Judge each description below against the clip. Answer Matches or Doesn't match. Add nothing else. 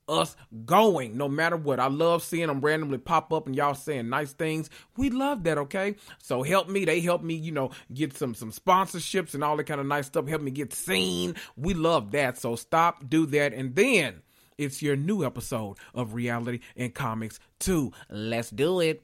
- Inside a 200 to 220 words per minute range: Matches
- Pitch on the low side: Doesn't match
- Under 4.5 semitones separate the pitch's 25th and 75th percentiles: Doesn't match